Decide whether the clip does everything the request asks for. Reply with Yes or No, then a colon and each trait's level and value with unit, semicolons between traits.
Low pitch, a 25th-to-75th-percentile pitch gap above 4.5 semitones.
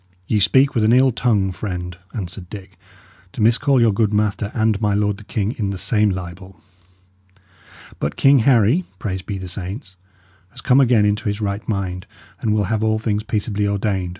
No: low, 105 Hz; narrow, 2.5 semitones